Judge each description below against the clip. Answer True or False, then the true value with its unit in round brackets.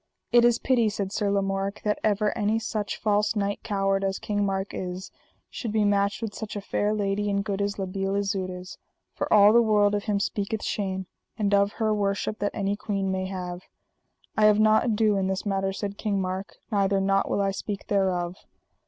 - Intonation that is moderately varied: False (1.4 semitones)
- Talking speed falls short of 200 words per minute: False (205 wpm)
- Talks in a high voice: True (200 Hz)